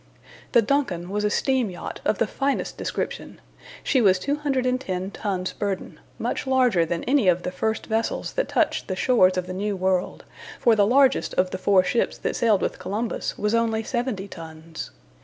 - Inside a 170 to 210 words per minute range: Yes, average, 180 wpm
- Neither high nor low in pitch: No, high, 210 Hz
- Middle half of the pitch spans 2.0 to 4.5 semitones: No, average, 5.2 semitones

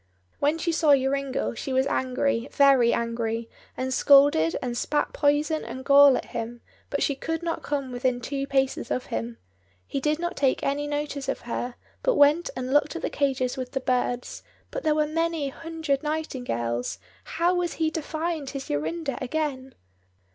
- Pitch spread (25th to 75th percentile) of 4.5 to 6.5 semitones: No, average, 3.2 semitones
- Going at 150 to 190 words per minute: Yes, average, 175 wpm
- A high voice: Yes, very high, 275 Hz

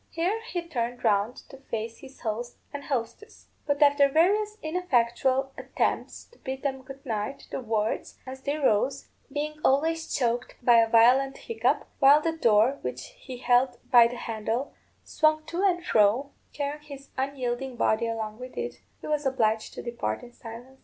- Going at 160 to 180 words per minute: Yes, average, 170 wpm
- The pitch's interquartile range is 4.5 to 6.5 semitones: No, average, 3.8 semitones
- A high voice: Yes, very high, 265 Hz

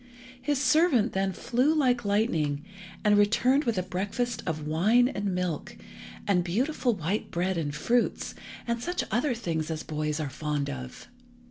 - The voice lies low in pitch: No, high, 200 Hz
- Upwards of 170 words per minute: No, average, 155 wpm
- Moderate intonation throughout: No, wide, 7.3 semitones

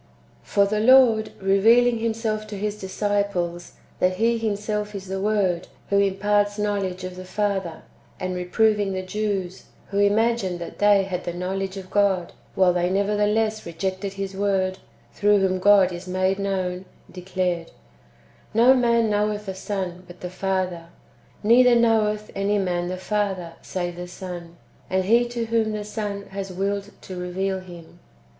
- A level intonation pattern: Yes, narrow, 2.3 semitones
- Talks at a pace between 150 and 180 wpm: Yes, average, 160 wpm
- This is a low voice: No, high, 195 Hz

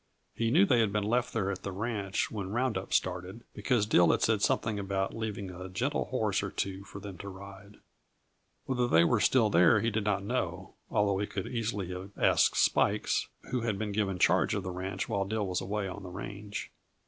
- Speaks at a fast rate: Yes, fast, 215 wpm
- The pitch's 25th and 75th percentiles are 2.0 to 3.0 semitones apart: Yes, narrow, 2.6 semitones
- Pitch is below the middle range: Yes, low, 100 Hz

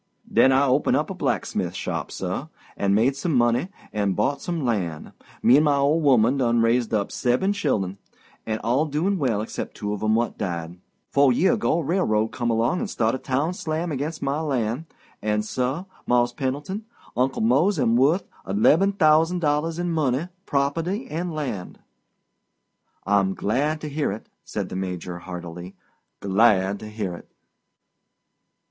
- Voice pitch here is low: Yes, low, 130 Hz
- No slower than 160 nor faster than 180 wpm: Yes, average, 165 wpm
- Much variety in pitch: Yes, wide, 6.3 semitones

